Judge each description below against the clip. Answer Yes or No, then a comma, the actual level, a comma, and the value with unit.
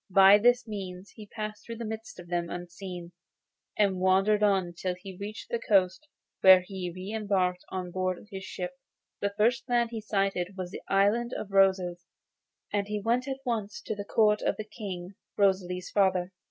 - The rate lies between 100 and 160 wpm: No, average, 180 wpm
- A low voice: No, high, 195 Hz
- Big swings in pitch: No, narrow, 2.6 semitones